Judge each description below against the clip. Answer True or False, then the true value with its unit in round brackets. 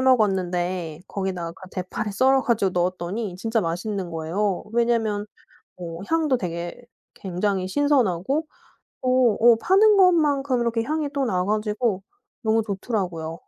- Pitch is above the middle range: True (210 Hz)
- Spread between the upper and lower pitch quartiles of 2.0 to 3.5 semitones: False (5.6 semitones)